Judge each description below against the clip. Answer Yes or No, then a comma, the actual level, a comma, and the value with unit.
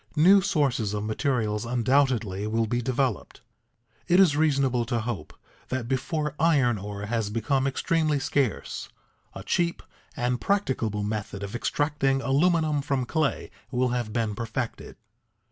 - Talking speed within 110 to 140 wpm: Yes, slow, 135 wpm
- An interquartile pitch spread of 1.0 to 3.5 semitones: No, average, 4.5 semitones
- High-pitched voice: No, low, 125 Hz